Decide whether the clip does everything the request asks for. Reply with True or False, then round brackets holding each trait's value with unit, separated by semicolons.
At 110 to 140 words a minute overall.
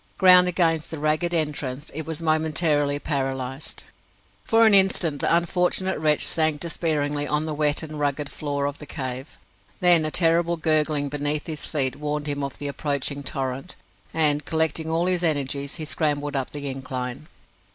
False (165 wpm)